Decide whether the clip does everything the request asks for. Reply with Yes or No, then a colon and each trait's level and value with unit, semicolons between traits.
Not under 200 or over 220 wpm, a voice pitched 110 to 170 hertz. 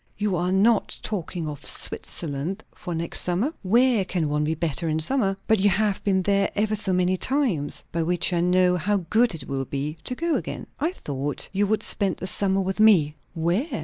No: fast, 205 wpm; medium, 185 Hz